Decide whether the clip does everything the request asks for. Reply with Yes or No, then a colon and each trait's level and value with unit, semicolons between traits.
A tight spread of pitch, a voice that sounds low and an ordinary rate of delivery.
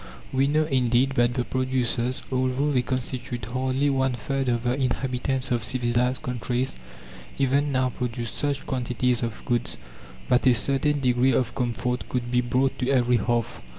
Yes: narrow, 1.6 semitones; low, 125 Hz; average, 160 wpm